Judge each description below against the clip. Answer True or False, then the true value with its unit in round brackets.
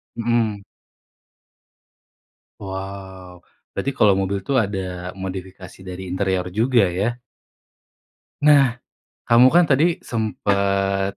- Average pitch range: True (3.7 semitones)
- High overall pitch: False (100 Hz)